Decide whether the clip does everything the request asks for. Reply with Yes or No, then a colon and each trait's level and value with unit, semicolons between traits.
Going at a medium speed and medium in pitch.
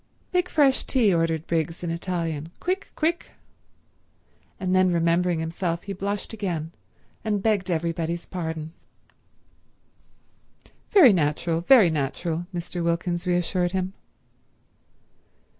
No: slow, 105 wpm; medium, 175 Hz